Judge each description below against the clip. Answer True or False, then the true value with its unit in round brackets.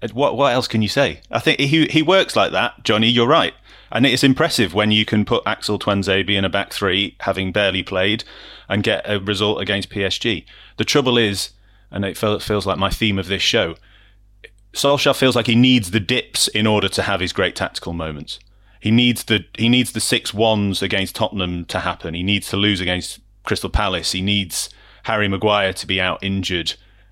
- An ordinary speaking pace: False (210 wpm)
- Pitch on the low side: True (105 Hz)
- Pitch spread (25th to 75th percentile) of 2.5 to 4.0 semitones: True (3.1 semitones)